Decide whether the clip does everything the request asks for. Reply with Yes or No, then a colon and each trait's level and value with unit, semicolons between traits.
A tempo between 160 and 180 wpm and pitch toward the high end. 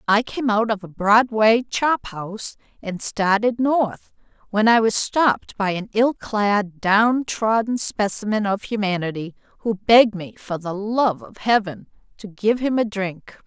Yes: average, 165 wpm; high, 210 Hz